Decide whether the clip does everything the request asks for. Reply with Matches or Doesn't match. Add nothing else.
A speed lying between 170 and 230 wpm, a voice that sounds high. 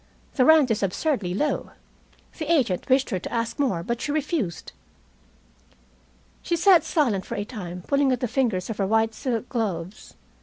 Matches